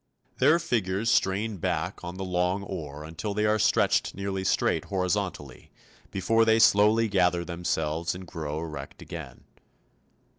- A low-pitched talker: Yes, very low, 95 Hz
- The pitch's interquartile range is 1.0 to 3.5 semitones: No, average, 4.1 semitones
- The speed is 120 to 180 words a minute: Yes, average, 140 wpm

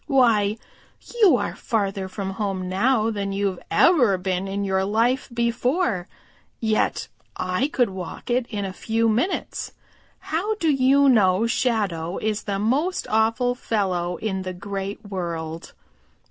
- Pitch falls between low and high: No, high, 210 Hz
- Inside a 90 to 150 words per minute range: Yes, average, 145 wpm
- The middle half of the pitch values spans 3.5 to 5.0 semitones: Yes, average, 4.4 semitones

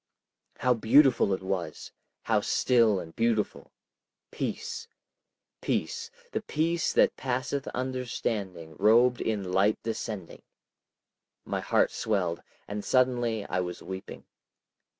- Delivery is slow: Yes, slow, 105 wpm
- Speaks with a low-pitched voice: Yes, low, 115 Hz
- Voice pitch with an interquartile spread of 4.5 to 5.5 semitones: Yes, average, 5.0 semitones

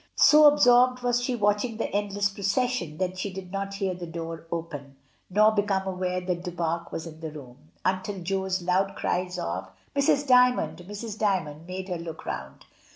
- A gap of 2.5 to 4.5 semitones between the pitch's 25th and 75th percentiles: Yes, average, 3.5 semitones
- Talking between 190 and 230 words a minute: No, average, 180 wpm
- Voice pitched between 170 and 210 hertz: Yes, high, 190 Hz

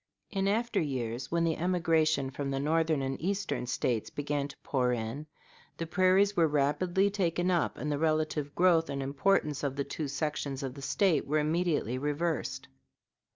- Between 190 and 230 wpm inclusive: No, average, 170 wpm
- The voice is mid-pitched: Yes, medium, 150 Hz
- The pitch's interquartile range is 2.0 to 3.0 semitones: No, average, 3.9 semitones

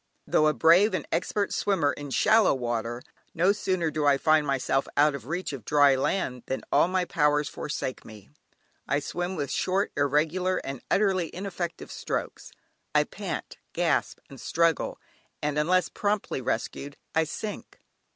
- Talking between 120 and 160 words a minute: Yes, average, 155 wpm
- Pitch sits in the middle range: Yes, medium, 150 Hz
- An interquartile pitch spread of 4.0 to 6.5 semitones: Yes, average, 4.8 semitones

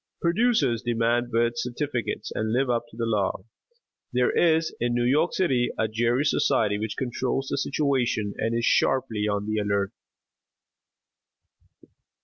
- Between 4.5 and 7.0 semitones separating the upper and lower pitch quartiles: No, average, 3.3 semitones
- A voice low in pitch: Yes, low, 120 Hz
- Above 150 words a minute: No, average, 140 wpm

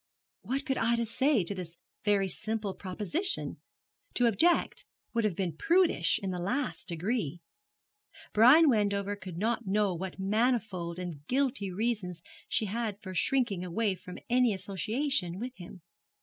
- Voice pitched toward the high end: Yes, high, 205 Hz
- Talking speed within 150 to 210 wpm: No, average, 140 wpm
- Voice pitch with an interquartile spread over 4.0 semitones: Yes, average, 4.7 semitones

